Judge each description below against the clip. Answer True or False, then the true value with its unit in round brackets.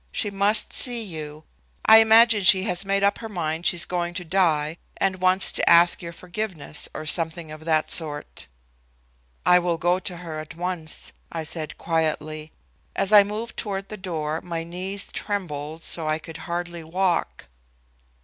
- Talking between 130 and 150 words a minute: False (170 wpm)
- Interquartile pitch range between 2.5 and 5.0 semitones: True (3.5 semitones)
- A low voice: False (175 Hz)